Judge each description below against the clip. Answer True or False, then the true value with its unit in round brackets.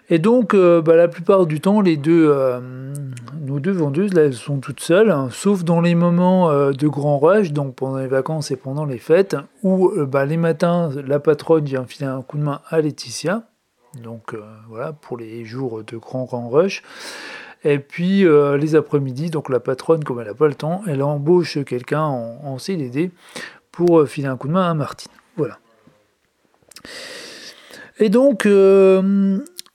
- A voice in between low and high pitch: True (150 Hz)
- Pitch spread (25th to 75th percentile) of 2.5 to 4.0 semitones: False (4.7 semitones)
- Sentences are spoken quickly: False (190 wpm)